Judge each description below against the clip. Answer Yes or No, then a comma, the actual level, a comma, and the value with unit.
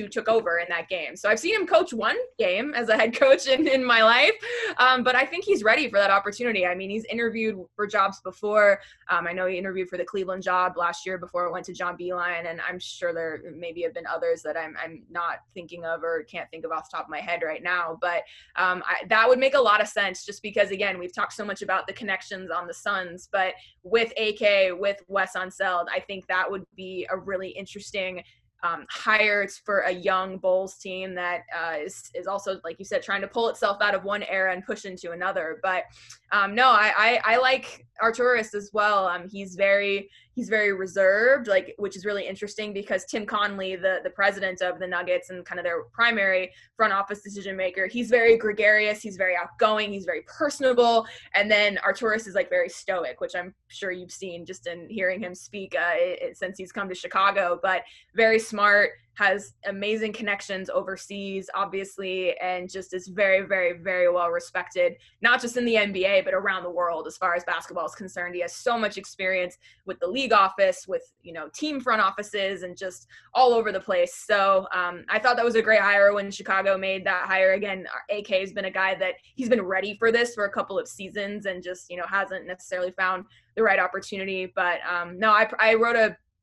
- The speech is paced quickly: Yes, fast, 220 wpm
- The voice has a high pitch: Yes, high, 195 Hz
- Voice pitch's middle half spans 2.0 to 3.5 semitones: Yes, average, 3.0 semitones